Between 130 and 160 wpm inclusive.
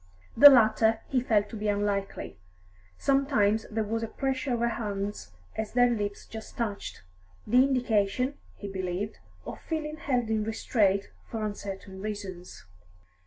Yes: average, 145 wpm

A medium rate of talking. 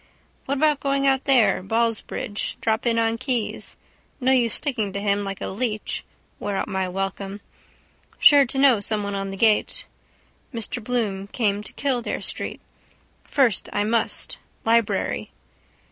Yes: average, 145 wpm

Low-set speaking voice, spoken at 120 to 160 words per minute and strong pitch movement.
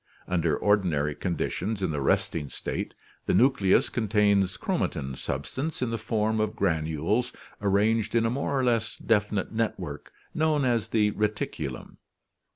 No: low, 105 Hz; average, 145 wpm; average, 4.1 semitones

